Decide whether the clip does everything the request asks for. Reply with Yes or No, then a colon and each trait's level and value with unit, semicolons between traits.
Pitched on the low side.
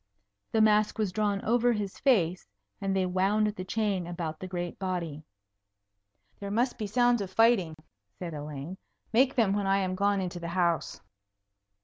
No: high, 195 Hz